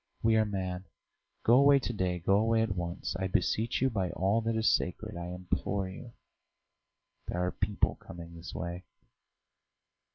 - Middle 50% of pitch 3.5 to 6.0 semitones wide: Yes, average, 3.8 semitones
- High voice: No, very low, 95 Hz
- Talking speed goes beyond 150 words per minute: Yes, average, 165 wpm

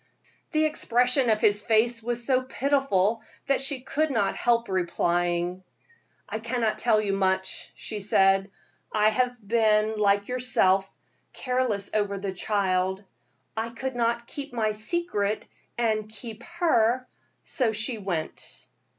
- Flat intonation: No, average, 3.7 semitones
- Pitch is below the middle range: No, high, 220 Hz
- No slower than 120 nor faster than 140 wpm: Yes, slow, 135 wpm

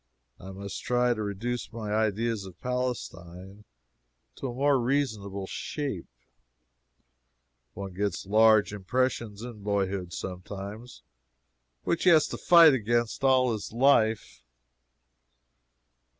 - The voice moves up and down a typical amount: Yes, average, 3.9 semitones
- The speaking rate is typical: No, slow, 110 wpm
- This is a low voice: Yes, low, 110 Hz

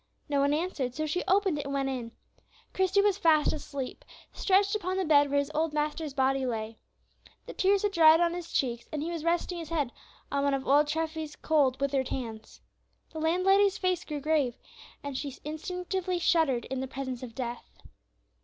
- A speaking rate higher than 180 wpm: Yes, average, 190 wpm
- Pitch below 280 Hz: No, very high, 300 Hz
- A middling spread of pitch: Yes, average, 4.3 semitones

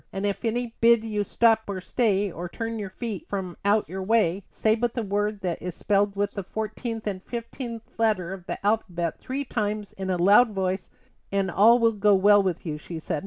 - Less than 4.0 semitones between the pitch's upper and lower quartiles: Yes, average, 3.0 semitones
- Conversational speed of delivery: No, fast, 215 wpm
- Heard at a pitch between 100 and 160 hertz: No, high, 205 Hz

